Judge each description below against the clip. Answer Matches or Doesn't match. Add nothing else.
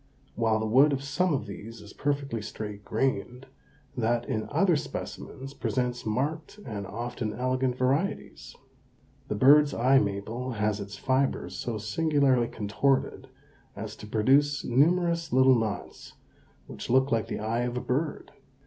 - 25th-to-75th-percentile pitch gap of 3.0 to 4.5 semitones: Matches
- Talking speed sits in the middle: Matches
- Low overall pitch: Matches